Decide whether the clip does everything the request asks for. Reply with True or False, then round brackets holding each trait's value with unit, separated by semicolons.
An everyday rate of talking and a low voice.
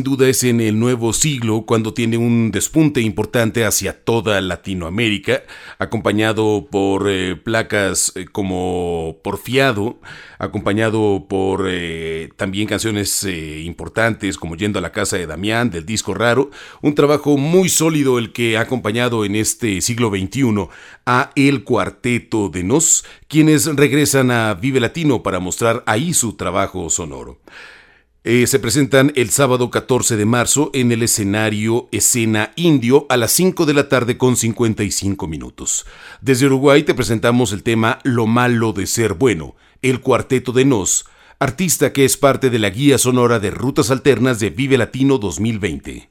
True (155 wpm; 115 Hz)